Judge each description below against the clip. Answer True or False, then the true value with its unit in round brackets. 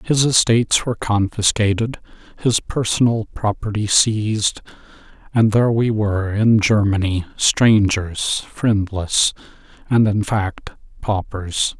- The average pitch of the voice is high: False (105 Hz)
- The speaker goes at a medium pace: False (100 wpm)